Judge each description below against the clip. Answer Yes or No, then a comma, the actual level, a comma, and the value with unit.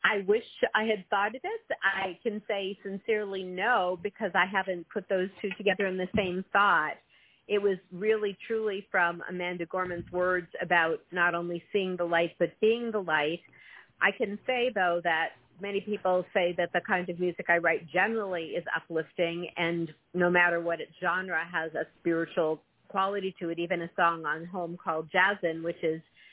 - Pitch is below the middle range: No, medium, 180 Hz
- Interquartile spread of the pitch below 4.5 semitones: Yes, average, 2.9 semitones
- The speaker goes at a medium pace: Yes, average, 180 wpm